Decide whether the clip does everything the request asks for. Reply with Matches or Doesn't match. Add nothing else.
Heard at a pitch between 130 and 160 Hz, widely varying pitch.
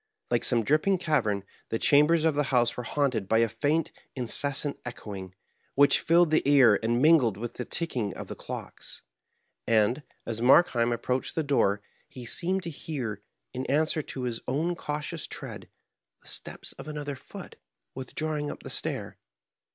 Doesn't match